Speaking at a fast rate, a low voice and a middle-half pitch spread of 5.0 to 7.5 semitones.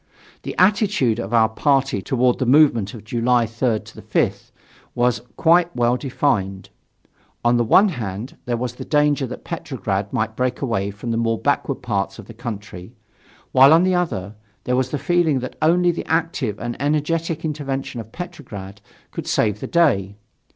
No: average, 170 wpm; low, 125 Hz; wide, 5.5 semitones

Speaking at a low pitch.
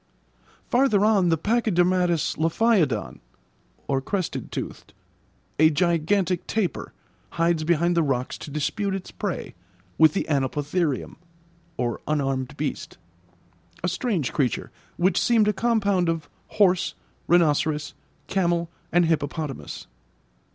No: medium, 170 Hz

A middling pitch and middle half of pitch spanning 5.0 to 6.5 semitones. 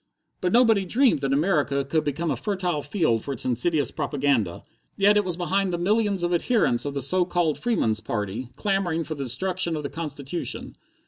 Yes: medium, 165 Hz; wide, 5.4 semitones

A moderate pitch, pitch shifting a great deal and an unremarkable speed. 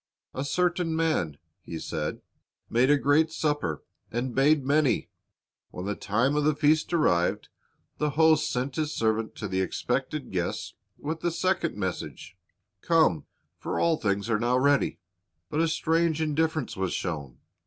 Yes: medium, 145 Hz; wide, 6.9 semitones; average, 155 wpm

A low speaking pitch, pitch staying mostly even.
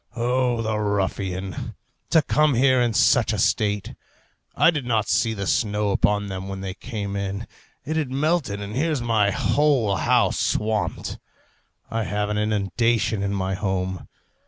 No: low, 105 Hz; average, 3.5 semitones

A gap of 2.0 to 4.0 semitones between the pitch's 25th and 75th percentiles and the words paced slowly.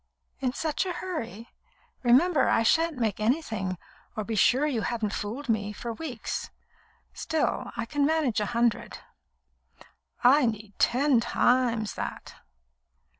No: average, 4.9 semitones; slow, 130 wpm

